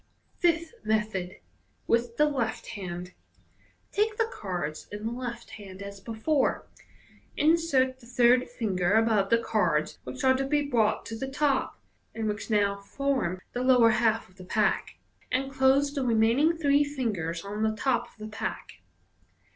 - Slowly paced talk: No, average, 165 wpm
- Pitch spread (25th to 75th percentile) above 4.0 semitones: Yes, average, 4.5 semitones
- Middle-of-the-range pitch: No, high, 230 Hz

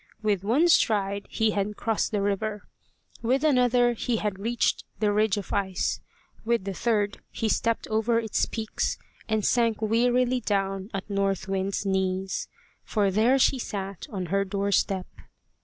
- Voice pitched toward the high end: Yes, high, 210 Hz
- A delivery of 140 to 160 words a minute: Yes, average, 155 wpm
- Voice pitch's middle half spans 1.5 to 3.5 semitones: Yes, average, 2.8 semitones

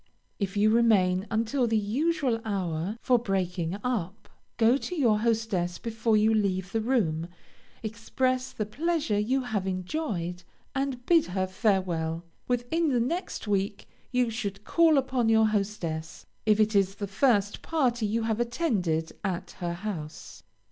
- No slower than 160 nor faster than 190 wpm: No, average, 150 wpm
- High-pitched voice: Yes, high, 215 Hz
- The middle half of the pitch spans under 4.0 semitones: No, average, 4.3 semitones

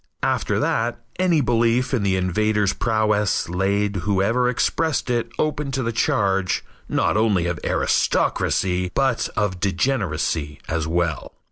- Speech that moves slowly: Yes, slow, 130 wpm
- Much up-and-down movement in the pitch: No, average, 4.4 semitones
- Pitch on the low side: Yes, low, 105 Hz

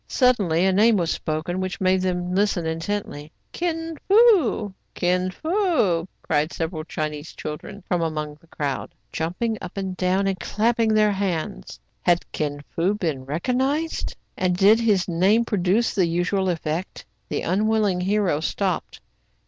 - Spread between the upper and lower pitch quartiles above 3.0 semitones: Yes, average, 4.3 semitones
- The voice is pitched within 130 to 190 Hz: Yes, medium, 185 Hz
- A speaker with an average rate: Yes, average, 155 wpm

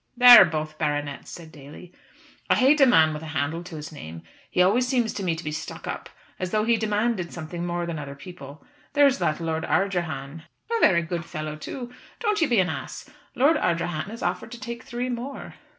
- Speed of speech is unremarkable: No, fast, 220 wpm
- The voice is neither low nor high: Yes, medium, 175 Hz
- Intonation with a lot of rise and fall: Yes, wide, 7.1 semitones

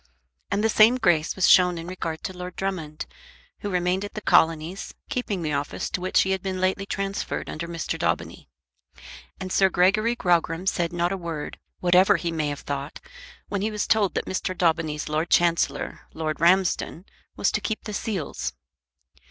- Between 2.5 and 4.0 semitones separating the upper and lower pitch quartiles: Yes, average, 2.9 semitones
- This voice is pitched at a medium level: Yes, medium, 180 Hz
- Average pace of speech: Yes, average, 180 wpm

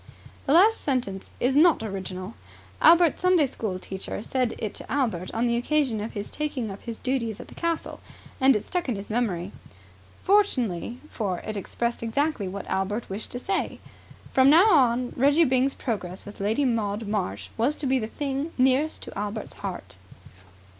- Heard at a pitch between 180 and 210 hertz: No, high, 235 Hz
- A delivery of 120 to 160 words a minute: No, average, 175 wpm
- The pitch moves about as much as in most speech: No, wide, 5.7 semitones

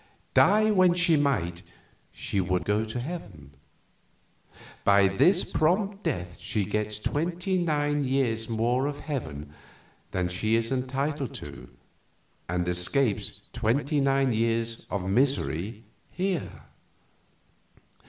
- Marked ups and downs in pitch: Yes, wide, 6.6 semitones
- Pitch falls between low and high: No, low, 125 Hz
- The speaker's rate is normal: No, slow, 115 wpm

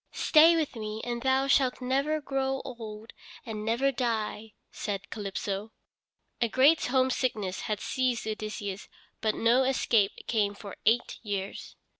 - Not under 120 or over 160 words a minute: Yes, slow, 135 wpm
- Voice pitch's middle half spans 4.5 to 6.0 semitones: No, average, 3.8 semitones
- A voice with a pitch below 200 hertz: No, high, 230 Hz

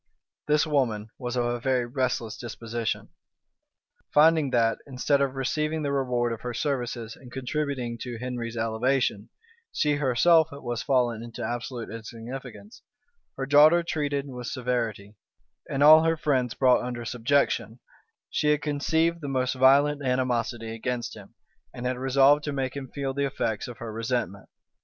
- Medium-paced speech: Yes, average, 150 wpm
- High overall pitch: No, low, 130 Hz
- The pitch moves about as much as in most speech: Yes, average, 3.1 semitones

